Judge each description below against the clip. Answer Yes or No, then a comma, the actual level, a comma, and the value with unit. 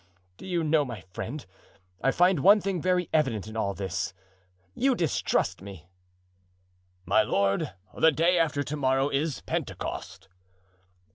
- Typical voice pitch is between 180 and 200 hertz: No, medium, 145 Hz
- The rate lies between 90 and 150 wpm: Yes, average, 140 wpm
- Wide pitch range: Yes, wide, 7.8 semitones